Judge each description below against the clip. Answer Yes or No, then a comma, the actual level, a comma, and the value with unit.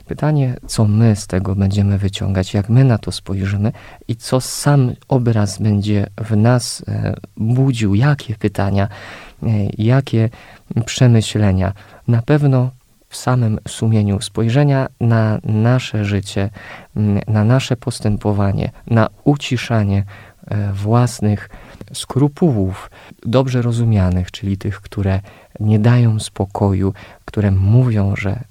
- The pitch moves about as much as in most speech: Yes, average, 3.6 semitones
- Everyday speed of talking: No, slow, 105 wpm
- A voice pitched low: Yes, low, 110 Hz